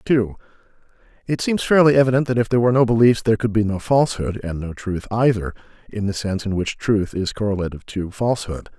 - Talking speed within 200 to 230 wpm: Yes, fast, 205 wpm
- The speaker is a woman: No, male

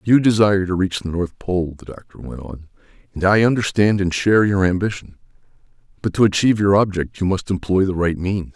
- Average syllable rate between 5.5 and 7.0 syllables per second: Yes, 5.8 syllables/s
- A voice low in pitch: Yes, very low, 95 Hz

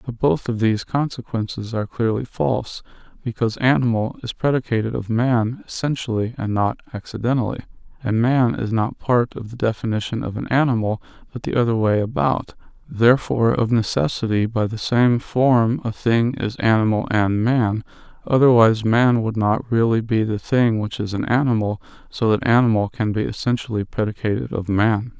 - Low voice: Yes, low, 115 Hz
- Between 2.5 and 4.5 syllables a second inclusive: No, 5.2 syllables/s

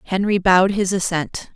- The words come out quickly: No, average, 155 wpm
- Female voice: Yes, female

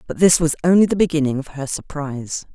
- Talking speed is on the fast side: Yes, fast, 215 wpm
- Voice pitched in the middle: Yes, medium, 155 Hz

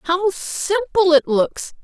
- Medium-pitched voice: No, very high, 355 Hz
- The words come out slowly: Yes, slow, 130 wpm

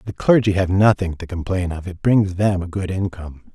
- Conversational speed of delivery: No, fast, 220 wpm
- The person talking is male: Yes, male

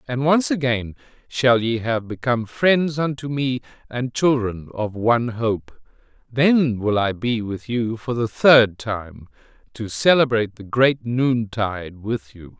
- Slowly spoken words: No, average, 150 wpm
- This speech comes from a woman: No, male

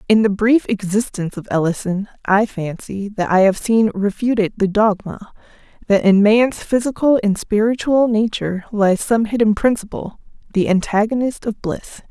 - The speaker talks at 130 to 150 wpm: Yes, average, 145 wpm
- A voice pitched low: No, high, 210 Hz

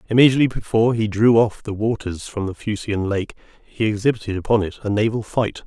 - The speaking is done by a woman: No, male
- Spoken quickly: No, average, 190 wpm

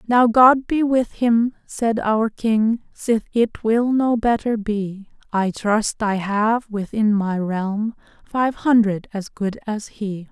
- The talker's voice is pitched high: Yes, high, 220 Hz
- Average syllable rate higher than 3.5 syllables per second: No, 3.4 syllables/s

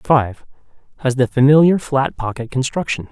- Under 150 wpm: Yes, slow, 135 wpm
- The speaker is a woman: No, male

